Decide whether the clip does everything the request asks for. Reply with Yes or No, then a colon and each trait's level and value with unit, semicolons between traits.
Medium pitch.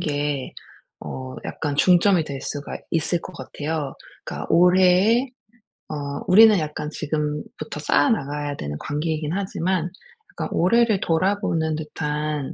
Yes: medium, 155 Hz